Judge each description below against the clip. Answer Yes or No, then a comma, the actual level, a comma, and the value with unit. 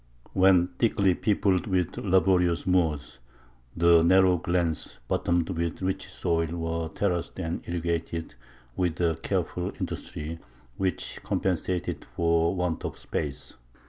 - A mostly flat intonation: Yes, narrow, 2.0 semitones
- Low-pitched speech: Yes, very low, 85 Hz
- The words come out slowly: Yes, slow, 115 wpm